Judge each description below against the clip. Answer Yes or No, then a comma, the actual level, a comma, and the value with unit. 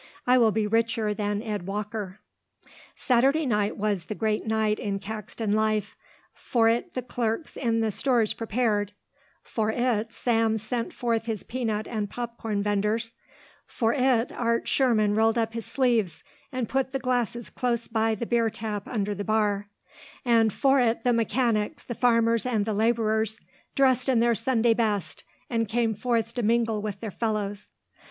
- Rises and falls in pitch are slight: Yes, narrow, 2.0 semitones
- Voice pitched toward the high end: Yes, high, 225 Hz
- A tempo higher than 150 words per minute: Yes, average, 165 wpm